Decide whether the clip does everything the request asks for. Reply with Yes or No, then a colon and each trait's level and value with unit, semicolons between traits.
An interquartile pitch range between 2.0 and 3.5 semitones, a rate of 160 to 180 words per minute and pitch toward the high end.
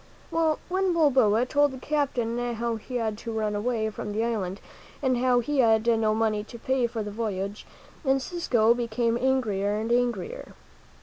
Yes: average, 3.1 semitones; average, 170 wpm; high, 235 Hz